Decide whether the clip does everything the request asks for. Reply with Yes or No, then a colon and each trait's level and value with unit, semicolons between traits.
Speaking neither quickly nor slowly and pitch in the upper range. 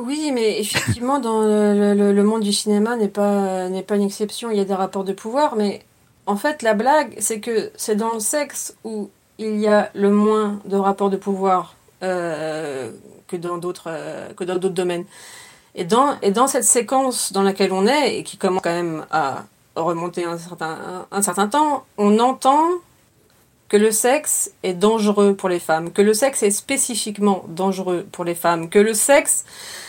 Yes: average, 195 wpm; high, 205 Hz